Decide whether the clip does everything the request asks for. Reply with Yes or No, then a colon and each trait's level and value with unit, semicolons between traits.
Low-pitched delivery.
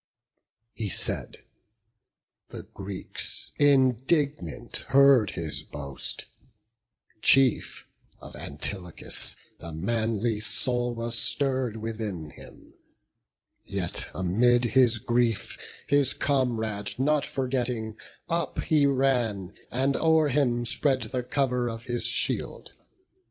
Yes: low, 120 Hz